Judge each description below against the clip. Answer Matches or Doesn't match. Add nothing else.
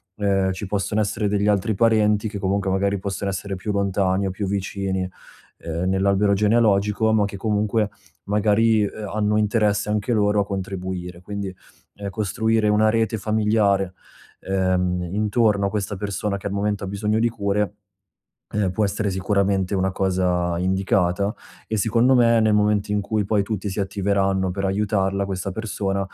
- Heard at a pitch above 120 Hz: Doesn't match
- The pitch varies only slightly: Matches